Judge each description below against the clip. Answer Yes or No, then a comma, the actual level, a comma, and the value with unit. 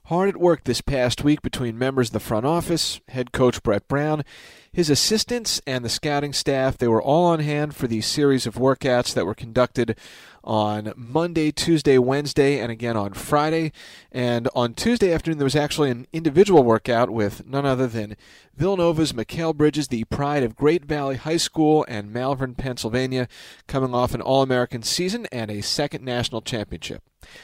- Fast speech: No, average, 175 wpm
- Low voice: Yes, low, 130 Hz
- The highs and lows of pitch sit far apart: No, average, 4.2 semitones